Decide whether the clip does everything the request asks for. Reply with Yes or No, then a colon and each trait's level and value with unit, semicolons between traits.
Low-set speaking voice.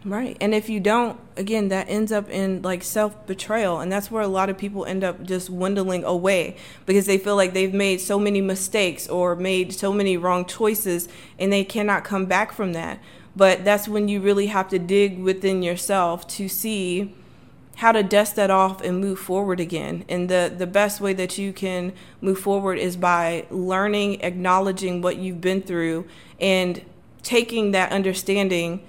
No: high, 190 Hz